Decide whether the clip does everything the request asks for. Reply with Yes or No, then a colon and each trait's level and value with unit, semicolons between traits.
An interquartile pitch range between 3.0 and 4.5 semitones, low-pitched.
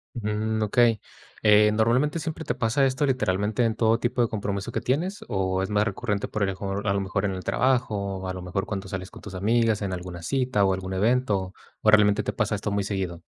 Yes: average, 3.3 semitones; low, 105 Hz